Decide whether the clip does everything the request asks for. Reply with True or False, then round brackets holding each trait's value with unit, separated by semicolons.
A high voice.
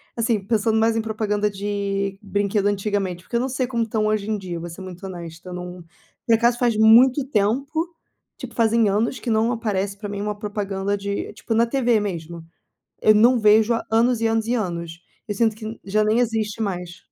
True (215 Hz)